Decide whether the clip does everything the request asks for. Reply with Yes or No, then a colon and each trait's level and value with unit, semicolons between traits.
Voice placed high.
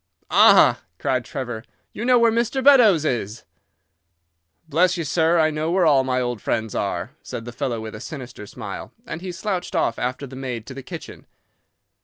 No: medium, 140 Hz